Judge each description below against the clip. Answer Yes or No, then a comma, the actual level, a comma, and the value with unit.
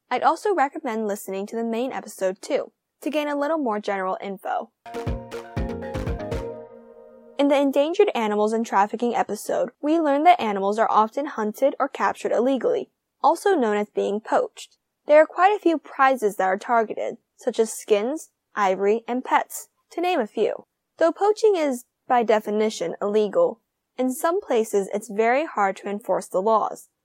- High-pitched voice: Yes, high, 240 Hz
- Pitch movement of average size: No, wide, 6.2 semitones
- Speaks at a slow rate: No, average, 160 wpm